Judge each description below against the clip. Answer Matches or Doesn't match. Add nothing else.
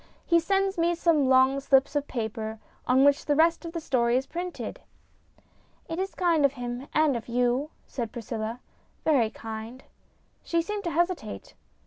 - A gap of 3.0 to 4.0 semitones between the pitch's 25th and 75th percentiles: Doesn't match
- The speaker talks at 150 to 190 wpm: Matches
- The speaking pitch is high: Matches